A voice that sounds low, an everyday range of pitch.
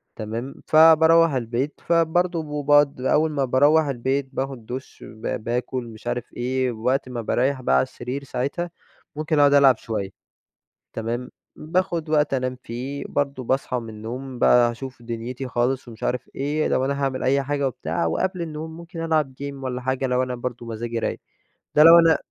Yes: low, 130 Hz; average, 3.5 semitones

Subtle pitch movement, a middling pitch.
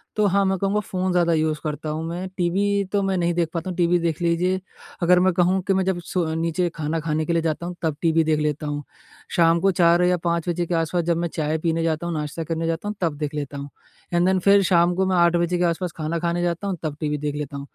Yes: narrow, 2.1 semitones; medium, 170 Hz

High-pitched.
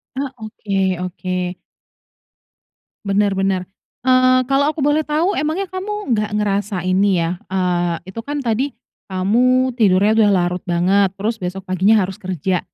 Yes: high, 205 Hz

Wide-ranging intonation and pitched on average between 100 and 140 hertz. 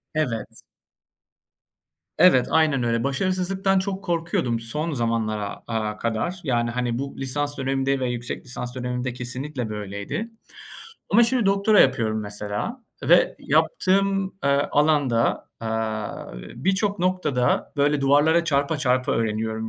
Yes: wide, 6.8 semitones; low, 135 Hz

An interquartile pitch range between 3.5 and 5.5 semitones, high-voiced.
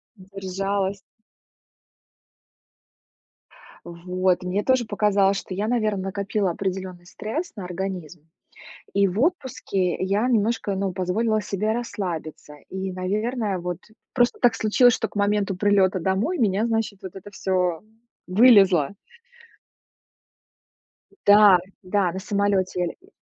No: narrow, 2.4 semitones; high, 195 Hz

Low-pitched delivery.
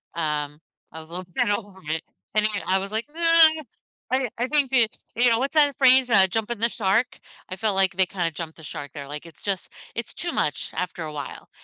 No: high, 195 Hz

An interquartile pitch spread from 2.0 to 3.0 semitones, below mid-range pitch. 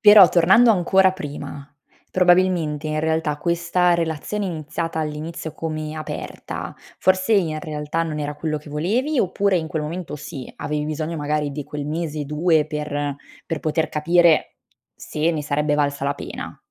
No: narrow, 2.6 semitones; medium, 155 Hz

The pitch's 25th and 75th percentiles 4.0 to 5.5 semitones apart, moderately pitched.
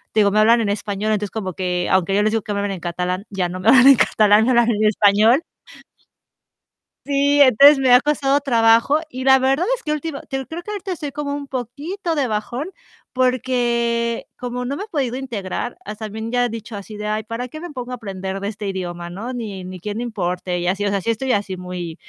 No: average, 4.7 semitones; high, 230 Hz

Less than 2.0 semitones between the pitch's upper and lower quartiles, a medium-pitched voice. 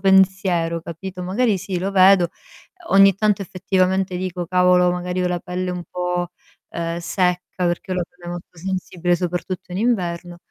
Yes: narrow, 1.3 semitones; medium, 180 Hz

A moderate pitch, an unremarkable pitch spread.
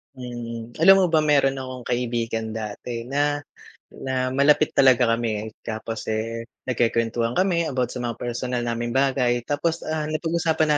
No: low, 125 Hz; average, 3.9 semitones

